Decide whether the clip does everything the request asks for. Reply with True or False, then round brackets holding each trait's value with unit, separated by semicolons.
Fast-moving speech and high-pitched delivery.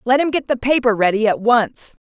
True (230 wpm; 240 Hz)